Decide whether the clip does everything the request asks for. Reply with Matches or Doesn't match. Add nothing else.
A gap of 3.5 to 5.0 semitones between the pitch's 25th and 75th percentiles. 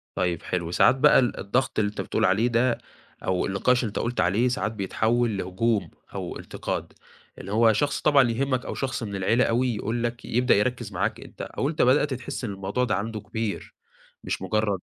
Matches